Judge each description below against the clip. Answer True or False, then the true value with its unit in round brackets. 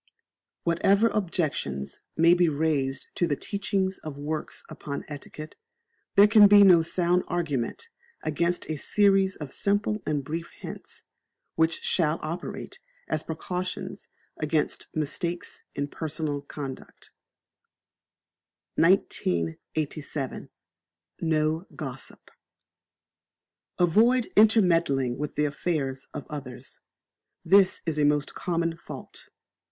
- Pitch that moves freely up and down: False (3.7 semitones)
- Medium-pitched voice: True (160 Hz)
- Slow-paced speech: True (105 wpm)